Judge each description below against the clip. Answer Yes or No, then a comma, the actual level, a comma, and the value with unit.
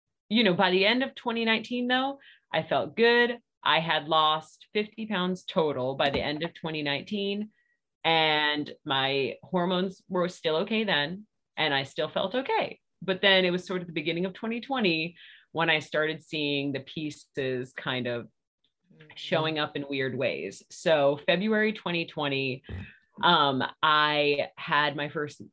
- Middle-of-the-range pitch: Yes, medium, 165 Hz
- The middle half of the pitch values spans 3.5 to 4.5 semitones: No, average, 5.3 semitones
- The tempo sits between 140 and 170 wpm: Yes, average, 155 wpm